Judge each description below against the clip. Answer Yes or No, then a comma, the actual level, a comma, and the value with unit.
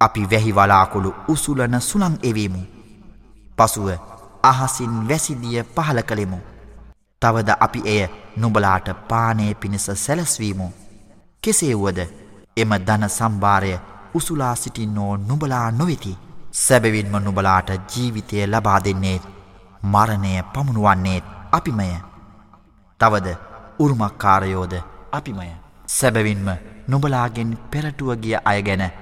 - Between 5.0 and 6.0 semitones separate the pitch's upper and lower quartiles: No, average, 3.4 semitones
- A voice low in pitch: Yes, low, 105 Hz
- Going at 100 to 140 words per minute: No, average, 85 wpm